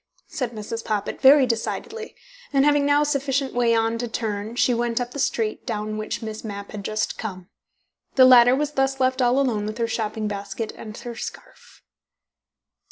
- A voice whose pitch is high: Yes, high, 235 Hz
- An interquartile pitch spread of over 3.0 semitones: Yes, average, 3.8 semitones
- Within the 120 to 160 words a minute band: No, average, 185 wpm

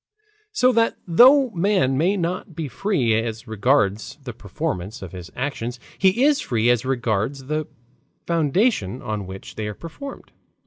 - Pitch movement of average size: No, wide, 8.9 semitones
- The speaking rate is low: No, average, 150 wpm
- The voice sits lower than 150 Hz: Yes, low, 135 Hz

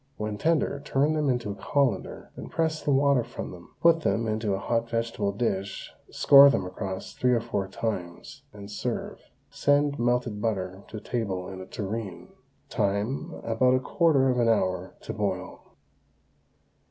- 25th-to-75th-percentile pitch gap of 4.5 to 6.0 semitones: Yes, average, 5.3 semitones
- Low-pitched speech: Yes, low, 115 Hz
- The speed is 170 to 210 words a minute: No, average, 160 wpm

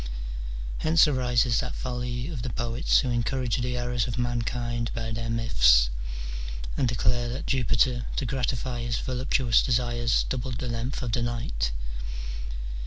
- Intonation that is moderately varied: No, narrow, 1.4 semitones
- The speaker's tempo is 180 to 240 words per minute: No, average, 145 wpm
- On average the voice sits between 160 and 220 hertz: No, low, 120 Hz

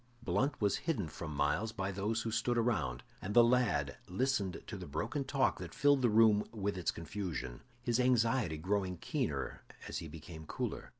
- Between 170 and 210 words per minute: Yes, average, 180 wpm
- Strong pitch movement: Yes, wide, 6.1 semitones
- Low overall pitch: Yes, low, 105 Hz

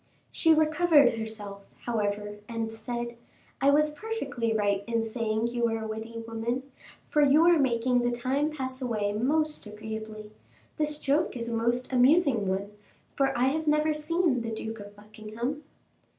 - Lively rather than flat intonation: No, average, 4.7 semitones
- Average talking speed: Yes, average, 160 wpm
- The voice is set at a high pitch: Yes, high, 235 Hz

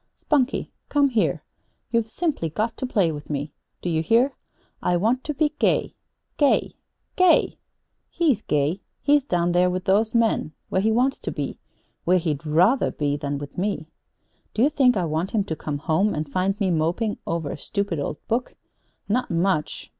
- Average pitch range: No, wide, 6.8 semitones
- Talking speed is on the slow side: No, average, 185 wpm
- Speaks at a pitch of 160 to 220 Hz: Yes, high, 190 Hz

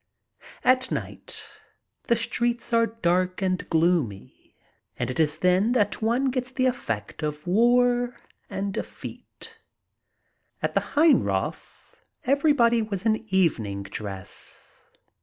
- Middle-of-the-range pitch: No, high, 210 Hz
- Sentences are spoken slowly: Yes, slow, 115 wpm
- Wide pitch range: Yes, wide, 7.0 semitones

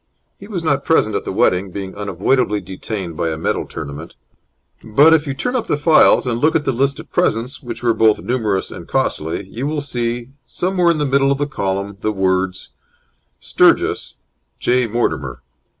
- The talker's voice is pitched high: No, low, 115 Hz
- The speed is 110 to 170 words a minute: No, average, 185 wpm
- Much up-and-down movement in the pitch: Yes, wide, 6.7 semitones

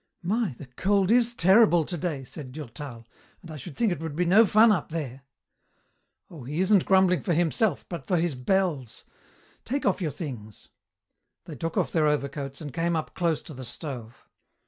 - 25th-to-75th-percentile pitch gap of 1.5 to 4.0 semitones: No, average, 5.1 semitones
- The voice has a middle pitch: Yes, medium, 165 Hz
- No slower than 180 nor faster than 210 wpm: Yes, average, 185 wpm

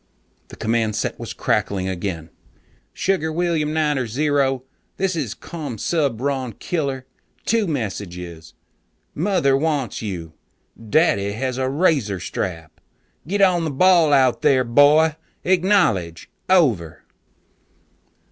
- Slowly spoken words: Yes, slow, 110 wpm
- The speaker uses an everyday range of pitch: No, wide, 7.5 semitones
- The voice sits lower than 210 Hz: Yes, low, 135 Hz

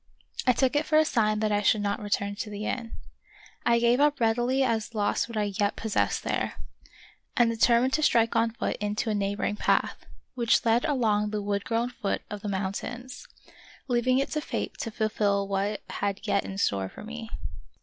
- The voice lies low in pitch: No, high, 220 Hz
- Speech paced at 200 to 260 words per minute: Yes, fast, 205 wpm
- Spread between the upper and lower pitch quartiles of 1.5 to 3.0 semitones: Yes, average, 2.7 semitones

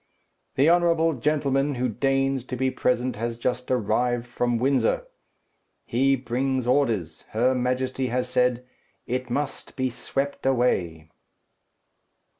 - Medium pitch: No, low, 125 Hz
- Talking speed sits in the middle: No, slow, 120 wpm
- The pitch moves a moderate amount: No, narrow, 2.0 semitones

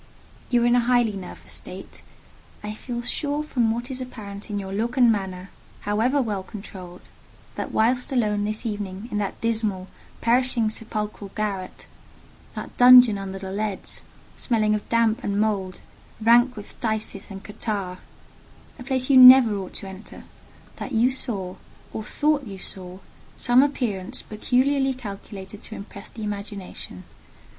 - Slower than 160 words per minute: Yes, average, 150 wpm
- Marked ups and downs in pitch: No, average, 3.5 semitones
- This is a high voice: Yes, high, 215 Hz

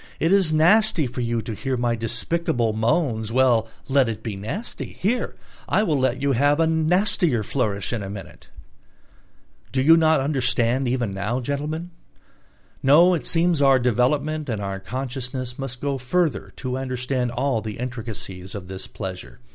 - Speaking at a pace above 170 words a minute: No, average, 165 wpm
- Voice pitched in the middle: No, low, 130 Hz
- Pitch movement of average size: Yes, average, 4.9 semitones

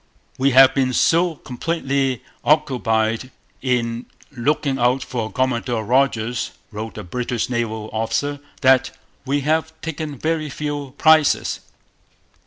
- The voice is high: No, low, 130 Hz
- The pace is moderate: No, slow, 115 wpm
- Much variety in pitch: No, average, 3.5 semitones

